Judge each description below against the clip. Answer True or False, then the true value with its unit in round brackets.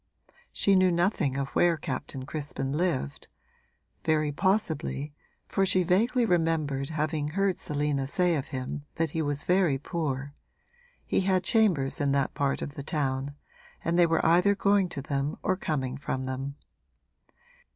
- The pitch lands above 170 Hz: False (155 Hz)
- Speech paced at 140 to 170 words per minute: True (150 wpm)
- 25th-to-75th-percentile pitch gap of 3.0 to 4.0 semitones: False (4.4 semitones)